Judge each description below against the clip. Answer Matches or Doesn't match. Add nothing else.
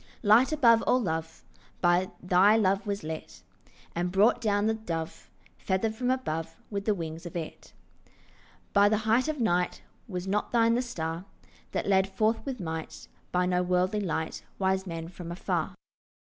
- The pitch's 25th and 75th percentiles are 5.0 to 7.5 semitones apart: Doesn't match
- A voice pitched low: Doesn't match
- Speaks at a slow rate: Doesn't match